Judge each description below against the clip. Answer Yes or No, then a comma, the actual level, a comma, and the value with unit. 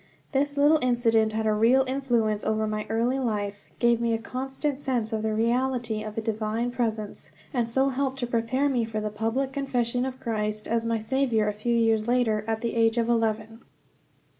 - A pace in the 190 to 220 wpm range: Yes, average, 195 wpm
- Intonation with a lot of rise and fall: No, narrow, 2.6 semitones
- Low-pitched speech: No, high, 230 Hz